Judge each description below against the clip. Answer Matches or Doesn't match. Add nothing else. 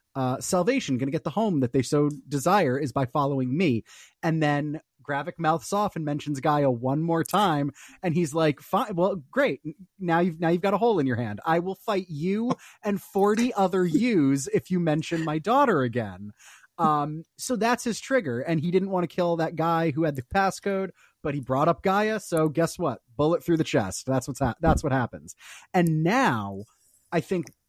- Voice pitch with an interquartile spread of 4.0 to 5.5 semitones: Matches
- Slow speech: Doesn't match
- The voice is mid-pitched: Matches